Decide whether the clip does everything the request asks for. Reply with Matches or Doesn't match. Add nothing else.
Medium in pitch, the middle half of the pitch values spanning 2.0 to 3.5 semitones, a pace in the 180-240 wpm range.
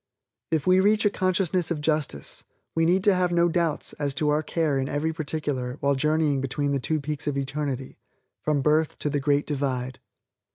Matches